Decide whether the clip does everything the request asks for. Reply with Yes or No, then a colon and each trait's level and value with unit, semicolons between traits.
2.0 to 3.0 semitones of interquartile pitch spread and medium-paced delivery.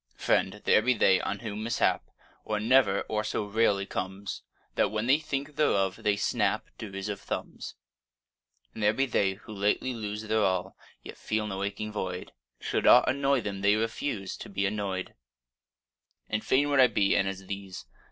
Yes: narrow, 2.5 semitones; average, 175 wpm